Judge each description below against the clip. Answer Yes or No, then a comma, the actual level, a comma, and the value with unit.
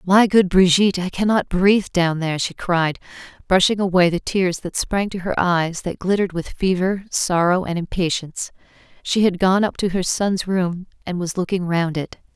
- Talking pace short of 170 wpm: No, average, 185 wpm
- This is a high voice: No, medium, 180 Hz